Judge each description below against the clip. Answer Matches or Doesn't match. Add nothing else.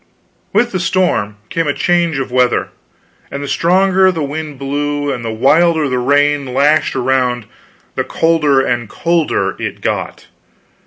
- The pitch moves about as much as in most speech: Matches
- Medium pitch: Matches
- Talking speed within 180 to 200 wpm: Doesn't match